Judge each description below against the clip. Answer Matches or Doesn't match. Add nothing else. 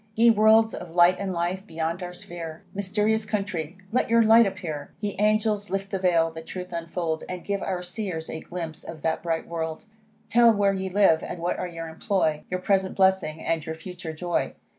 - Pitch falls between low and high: Matches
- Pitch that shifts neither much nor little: Matches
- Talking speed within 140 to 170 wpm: Doesn't match